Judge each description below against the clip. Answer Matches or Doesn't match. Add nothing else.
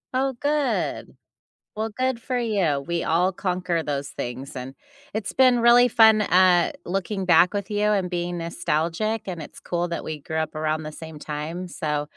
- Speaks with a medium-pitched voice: Matches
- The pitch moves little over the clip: Doesn't match